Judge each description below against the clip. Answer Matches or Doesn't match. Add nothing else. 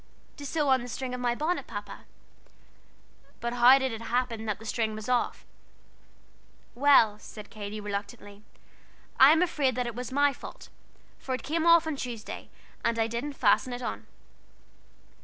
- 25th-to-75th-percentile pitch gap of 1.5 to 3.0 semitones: Doesn't match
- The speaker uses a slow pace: Doesn't match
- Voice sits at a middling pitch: Doesn't match